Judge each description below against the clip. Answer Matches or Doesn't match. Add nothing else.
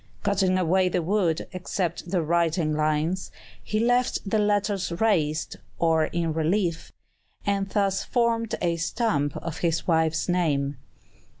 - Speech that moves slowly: Matches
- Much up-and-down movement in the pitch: Doesn't match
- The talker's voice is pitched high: Doesn't match